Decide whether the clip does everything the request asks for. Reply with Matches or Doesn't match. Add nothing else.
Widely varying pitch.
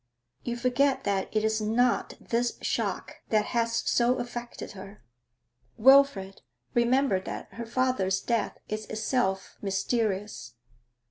Doesn't match